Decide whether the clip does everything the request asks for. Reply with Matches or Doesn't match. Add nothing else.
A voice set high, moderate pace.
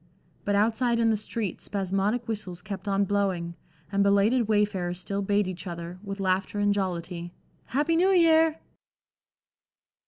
Matches